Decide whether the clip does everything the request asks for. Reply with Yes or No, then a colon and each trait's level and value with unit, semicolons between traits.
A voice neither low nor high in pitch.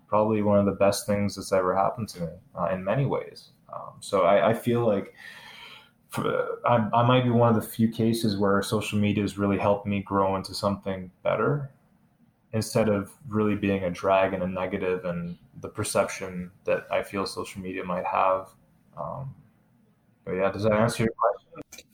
No: low, 100 Hz